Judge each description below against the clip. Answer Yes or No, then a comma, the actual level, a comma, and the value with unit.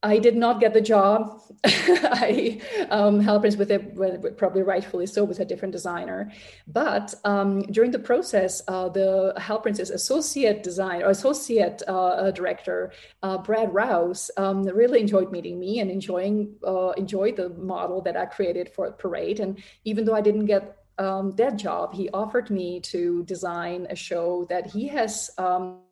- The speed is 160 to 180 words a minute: Yes, average, 170 wpm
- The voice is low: No, high, 195 Hz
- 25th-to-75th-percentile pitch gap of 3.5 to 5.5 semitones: No, average, 2.7 semitones